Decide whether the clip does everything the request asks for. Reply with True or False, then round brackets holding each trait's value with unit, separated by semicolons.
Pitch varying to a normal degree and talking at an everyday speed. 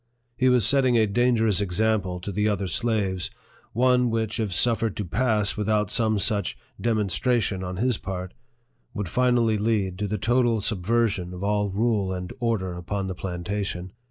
True (3.5 semitones; 170 wpm)